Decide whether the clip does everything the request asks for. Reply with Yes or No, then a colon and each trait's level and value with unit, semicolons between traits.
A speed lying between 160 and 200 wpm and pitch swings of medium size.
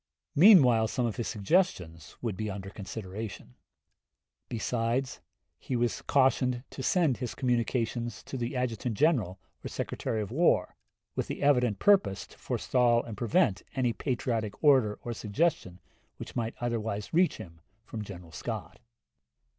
No: average, 140 wpm; average, 3.8 semitones